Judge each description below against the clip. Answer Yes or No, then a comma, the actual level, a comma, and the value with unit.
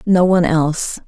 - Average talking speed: Yes, average, 165 wpm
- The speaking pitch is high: No, medium, 170 Hz